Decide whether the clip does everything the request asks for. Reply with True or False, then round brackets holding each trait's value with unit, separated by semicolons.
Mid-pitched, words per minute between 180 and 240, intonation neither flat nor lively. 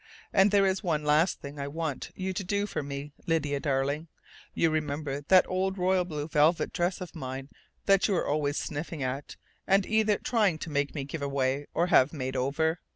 True (155 Hz; 200 wpm; 4.5 semitones)